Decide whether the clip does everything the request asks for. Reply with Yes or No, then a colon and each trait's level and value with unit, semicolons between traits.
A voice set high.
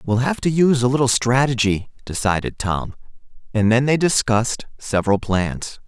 No: low, 120 Hz